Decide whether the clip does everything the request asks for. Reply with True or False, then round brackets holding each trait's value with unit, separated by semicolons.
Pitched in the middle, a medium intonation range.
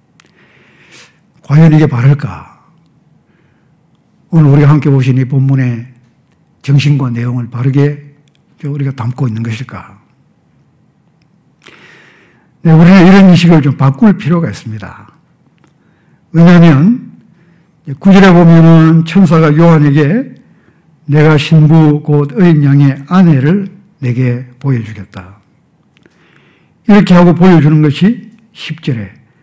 True (150 Hz; 4.0 semitones)